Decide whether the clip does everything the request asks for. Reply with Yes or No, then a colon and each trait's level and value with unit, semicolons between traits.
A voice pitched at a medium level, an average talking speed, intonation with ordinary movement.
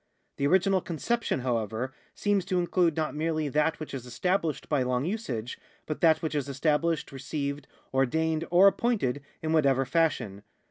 Yes: medium, 155 Hz; average, 155 wpm; average, 4.0 semitones